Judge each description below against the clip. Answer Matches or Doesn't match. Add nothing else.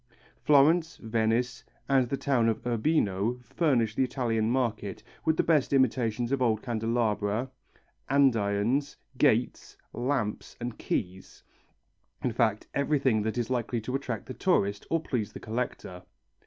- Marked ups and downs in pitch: Doesn't match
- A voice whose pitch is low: Matches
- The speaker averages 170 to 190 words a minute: Doesn't match